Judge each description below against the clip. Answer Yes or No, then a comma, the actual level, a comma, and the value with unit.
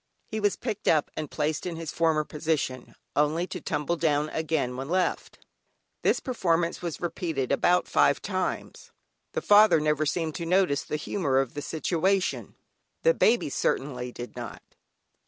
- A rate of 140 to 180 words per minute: Yes, average, 155 wpm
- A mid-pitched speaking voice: Yes, medium, 160 Hz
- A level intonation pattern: No, average, 3.5 semitones